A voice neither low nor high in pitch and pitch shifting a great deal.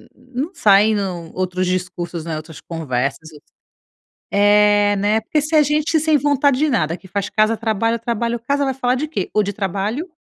No: high, 210 Hz; wide, 6.2 semitones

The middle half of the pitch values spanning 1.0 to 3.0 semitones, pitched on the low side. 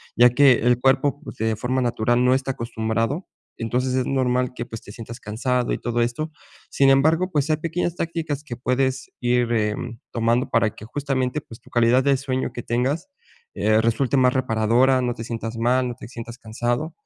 Yes: narrow, 2.5 semitones; low, 125 Hz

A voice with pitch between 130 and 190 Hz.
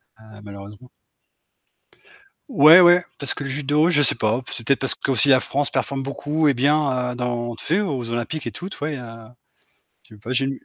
Yes: low, 135 Hz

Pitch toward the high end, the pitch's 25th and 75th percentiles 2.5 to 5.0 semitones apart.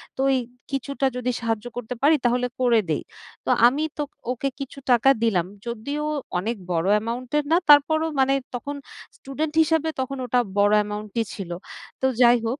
Yes: very high, 250 Hz; average, 3.7 semitones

